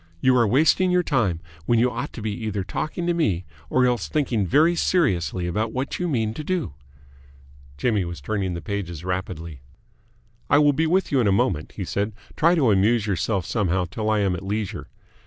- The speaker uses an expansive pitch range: Yes, wide, 7.0 semitones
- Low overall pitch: Yes, low, 110 Hz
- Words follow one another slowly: No, average, 200 wpm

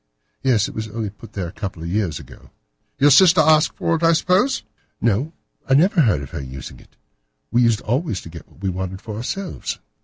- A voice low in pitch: Yes, low, 110 Hz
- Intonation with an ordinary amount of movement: No, wide, 8.5 semitones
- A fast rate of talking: Yes, fast, 215 wpm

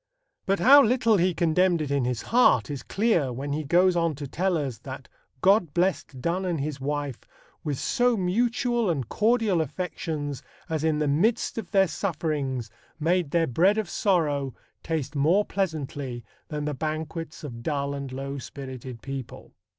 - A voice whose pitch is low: No, medium, 155 Hz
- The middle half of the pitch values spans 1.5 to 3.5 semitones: No, average, 5.0 semitones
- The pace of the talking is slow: No, average, 165 wpm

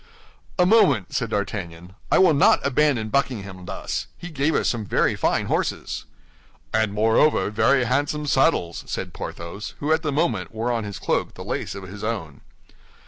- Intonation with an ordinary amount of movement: No, wide, 6.3 semitones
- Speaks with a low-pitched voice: Yes, low, 115 Hz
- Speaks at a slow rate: No, average, 170 wpm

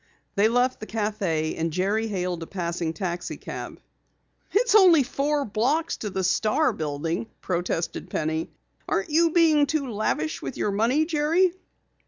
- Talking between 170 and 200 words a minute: No, average, 145 wpm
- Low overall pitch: No, high, 215 Hz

